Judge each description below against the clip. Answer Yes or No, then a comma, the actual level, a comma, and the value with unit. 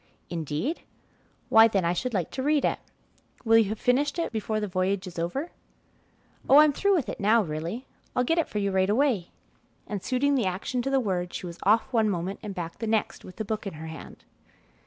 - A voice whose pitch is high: Yes, high, 215 Hz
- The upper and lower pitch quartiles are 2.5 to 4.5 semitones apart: No, wide, 5.6 semitones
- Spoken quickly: Yes, fast, 225 wpm